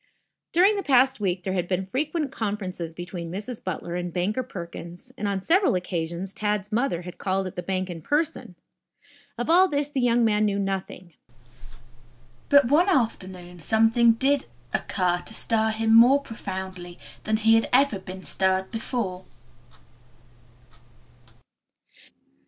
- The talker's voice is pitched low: No, high, 205 Hz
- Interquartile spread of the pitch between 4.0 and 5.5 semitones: Yes, average, 5.0 semitones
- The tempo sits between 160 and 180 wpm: No, average, 145 wpm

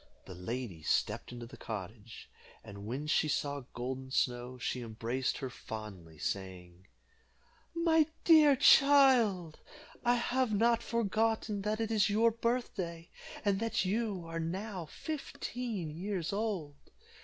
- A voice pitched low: No, medium, 175 Hz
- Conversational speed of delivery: No, slow, 130 wpm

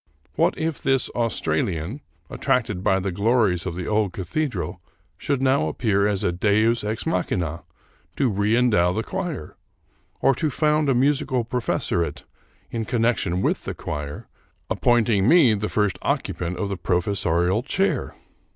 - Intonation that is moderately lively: No, wide, 5.7 semitones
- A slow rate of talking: No, average, 150 wpm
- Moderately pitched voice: No, low, 105 Hz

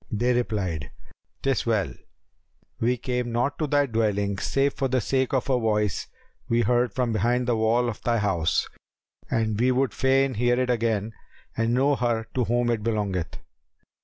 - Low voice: Yes, low, 120 Hz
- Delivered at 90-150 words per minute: No, average, 170 wpm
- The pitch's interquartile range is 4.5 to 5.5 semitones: No, narrow, 2.5 semitones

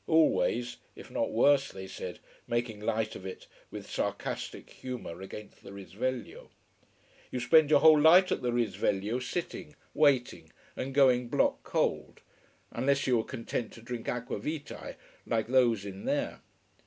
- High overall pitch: No, low, 125 Hz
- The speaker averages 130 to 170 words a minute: Yes, average, 150 wpm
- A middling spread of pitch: Yes, average, 4.0 semitones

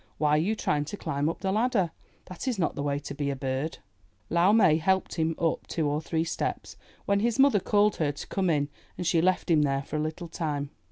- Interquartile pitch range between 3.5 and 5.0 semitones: Yes, average, 4.5 semitones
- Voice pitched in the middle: Yes, medium, 165 Hz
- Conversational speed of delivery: No, fast, 240 wpm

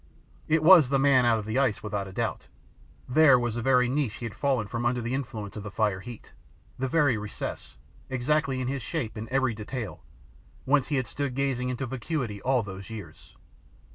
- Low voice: Yes, low, 125 Hz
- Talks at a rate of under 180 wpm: No, average, 200 wpm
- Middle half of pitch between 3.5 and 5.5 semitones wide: Yes, average, 3.8 semitones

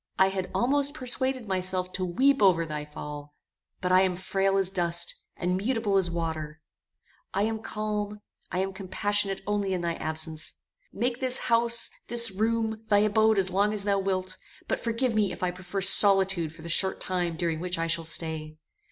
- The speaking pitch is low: No, high, 190 Hz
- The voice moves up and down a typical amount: Yes, average, 3.6 semitones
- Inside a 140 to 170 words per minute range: No, average, 185 wpm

